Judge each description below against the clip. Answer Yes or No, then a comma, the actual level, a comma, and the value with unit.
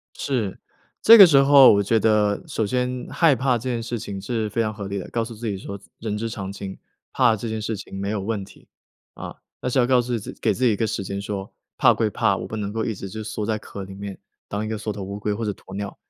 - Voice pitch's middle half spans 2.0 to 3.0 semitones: Yes, average, 2.7 semitones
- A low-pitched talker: Yes, low, 110 Hz